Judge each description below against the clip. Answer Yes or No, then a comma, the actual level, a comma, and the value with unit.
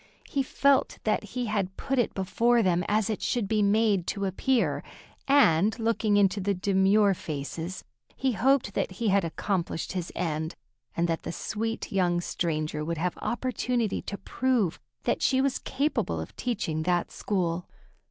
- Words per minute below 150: No, average, 160 wpm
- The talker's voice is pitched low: No, high, 200 Hz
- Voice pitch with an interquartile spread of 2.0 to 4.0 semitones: No, average, 4.7 semitones